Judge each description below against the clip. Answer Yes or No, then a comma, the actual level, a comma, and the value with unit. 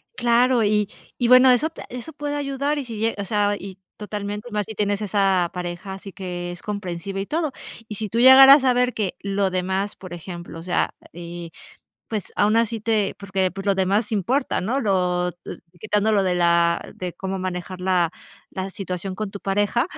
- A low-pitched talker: No, high, 200 Hz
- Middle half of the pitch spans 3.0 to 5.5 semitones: Yes, average, 3.6 semitones